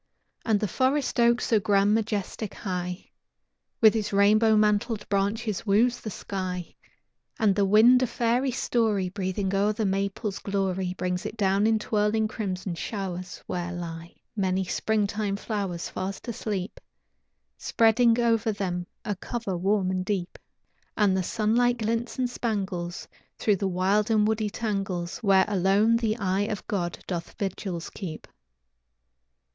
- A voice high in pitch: Yes, high, 205 Hz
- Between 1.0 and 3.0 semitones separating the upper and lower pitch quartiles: Yes, average, 2.7 semitones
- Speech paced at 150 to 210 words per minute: No, average, 140 wpm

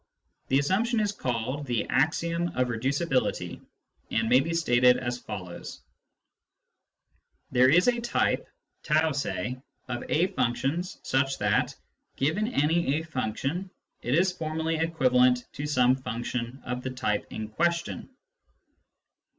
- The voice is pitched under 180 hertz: Yes, low, 135 Hz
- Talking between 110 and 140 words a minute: Yes, slow, 135 wpm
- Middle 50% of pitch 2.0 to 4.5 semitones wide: No, average, 5.0 semitones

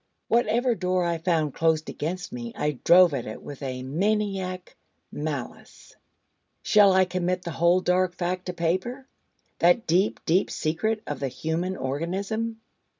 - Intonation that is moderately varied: Yes, average, 3.3 semitones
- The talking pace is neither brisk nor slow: Yes, average, 150 wpm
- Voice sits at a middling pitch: Yes, medium, 180 Hz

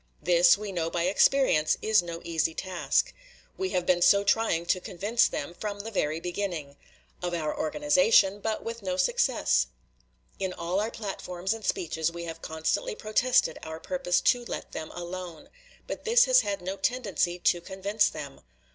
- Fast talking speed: No, average, 170 wpm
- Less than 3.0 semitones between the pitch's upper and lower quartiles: No, average, 4.0 semitones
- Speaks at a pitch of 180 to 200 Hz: Yes, medium, 185 Hz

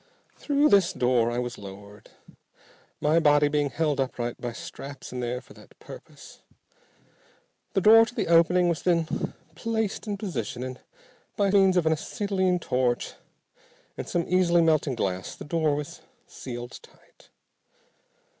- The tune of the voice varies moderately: No, wide, 6.7 semitones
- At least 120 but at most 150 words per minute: Yes, average, 145 wpm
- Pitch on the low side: No, medium, 155 Hz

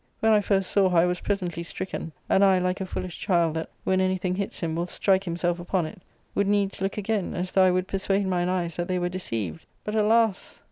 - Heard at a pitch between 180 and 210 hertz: Yes, medium, 185 Hz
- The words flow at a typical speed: No, fast, 250 wpm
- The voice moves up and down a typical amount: No, narrow, 2.0 semitones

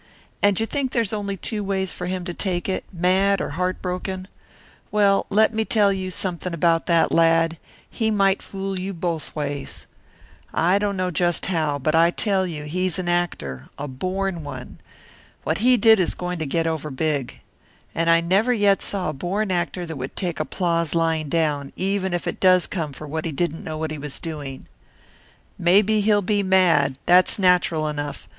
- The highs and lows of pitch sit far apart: No, average, 3.5 semitones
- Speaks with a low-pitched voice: No, medium, 180 Hz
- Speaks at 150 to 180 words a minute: No, average, 190 wpm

